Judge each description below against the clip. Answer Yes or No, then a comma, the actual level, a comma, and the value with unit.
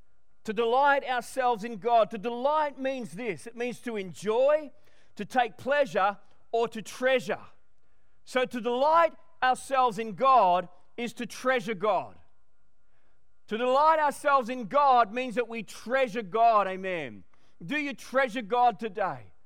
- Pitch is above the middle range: Yes, high, 245 Hz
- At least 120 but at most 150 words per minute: Yes, average, 140 wpm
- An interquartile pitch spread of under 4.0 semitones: Yes, average, 3.2 semitones